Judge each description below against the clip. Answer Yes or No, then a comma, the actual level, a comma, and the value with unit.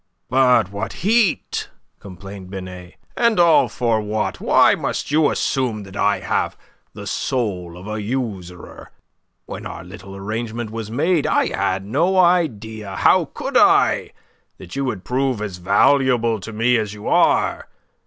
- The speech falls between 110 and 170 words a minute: Yes, average, 150 wpm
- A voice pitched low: Yes, low, 110 Hz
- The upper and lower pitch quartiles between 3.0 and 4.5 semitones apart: No, average, 5.0 semitones